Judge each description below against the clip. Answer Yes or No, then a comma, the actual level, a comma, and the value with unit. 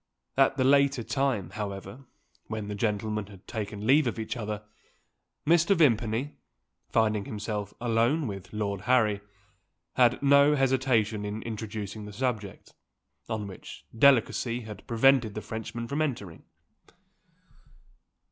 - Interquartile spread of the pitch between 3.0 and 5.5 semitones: Yes, average, 4.0 semitones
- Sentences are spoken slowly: Yes, slow, 125 wpm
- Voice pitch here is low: Yes, low, 110 Hz